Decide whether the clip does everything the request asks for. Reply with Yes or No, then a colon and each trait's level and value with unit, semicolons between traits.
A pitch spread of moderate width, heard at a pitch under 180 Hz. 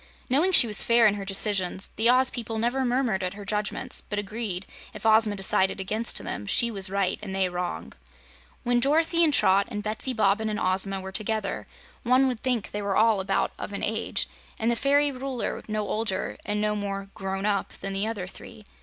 No: average, 3.2 semitones; high, 210 Hz